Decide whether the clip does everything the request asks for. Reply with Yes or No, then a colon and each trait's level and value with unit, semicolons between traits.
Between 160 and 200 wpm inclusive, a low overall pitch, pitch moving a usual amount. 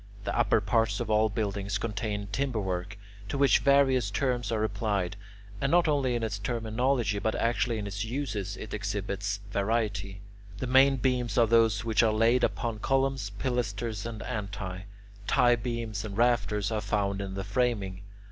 Yes: average, 165 wpm; low, 110 Hz; average, 3.1 semitones